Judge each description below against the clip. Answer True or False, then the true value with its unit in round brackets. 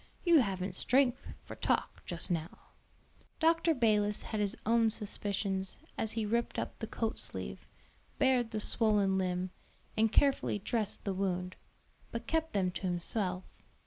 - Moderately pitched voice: False (210 Hz)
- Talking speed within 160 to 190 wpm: False (145 wpm)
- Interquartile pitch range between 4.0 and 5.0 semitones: False (3.6 semitones)